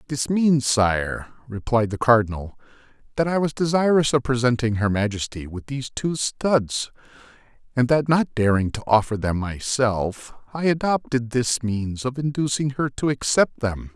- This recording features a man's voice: Yes, male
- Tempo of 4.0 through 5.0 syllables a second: Yes, 4.6 syllables/s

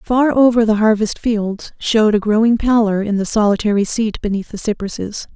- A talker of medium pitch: No, high, 215 Hz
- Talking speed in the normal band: Yes, average, 180 wpm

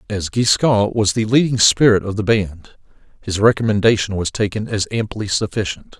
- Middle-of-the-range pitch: No, low, 105 Hz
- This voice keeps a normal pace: Yes, average, 160 wpm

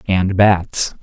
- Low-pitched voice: Yes, very low, 95 Hz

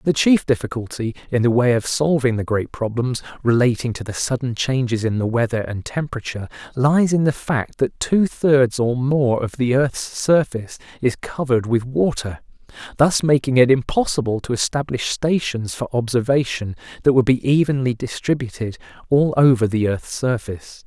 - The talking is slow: No, average, 165 wpm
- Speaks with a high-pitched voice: No, low, 125 Hz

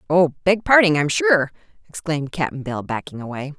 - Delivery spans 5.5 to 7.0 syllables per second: No, 5.2 syllables/s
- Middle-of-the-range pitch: Yes, medium, 160 Hz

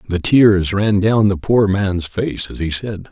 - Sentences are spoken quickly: Yes, fast, 210 wpm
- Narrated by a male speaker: Yes, male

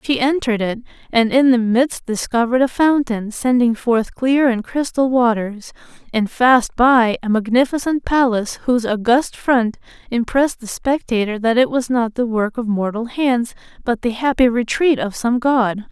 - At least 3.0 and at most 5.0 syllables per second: Yes, 4.7 syllables/s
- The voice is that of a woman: Yes, female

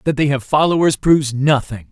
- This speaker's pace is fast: No, average, 190 wpm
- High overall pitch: No, medium, 140 Hz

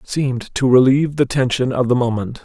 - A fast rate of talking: No, average, 195 wpm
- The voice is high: No, low, 130 Hz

